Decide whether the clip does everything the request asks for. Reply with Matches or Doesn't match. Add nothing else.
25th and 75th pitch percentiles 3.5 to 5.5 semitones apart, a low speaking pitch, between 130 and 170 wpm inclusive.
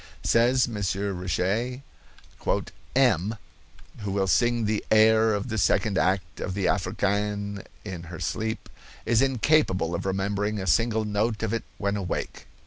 Doesn't match